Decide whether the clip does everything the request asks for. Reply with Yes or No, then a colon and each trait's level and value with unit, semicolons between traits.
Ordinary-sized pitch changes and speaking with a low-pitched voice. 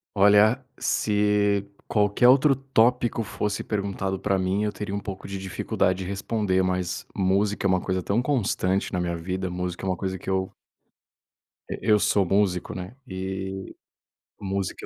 No: narrow, 1.9 semitones; low, 100 Hz